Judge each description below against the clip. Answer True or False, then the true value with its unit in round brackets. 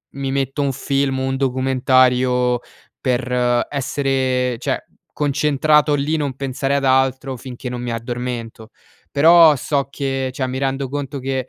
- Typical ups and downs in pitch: False (1.7 semitones)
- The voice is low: True (130 Hz)